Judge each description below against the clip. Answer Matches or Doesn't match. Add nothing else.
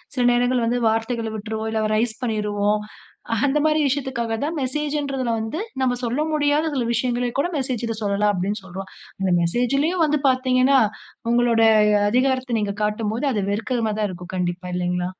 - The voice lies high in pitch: Matches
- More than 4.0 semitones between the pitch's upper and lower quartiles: Doesn't match